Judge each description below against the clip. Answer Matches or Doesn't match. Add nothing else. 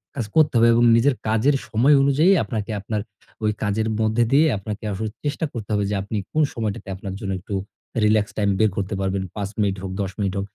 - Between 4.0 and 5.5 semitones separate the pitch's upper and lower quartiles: Doesn't match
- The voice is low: Matches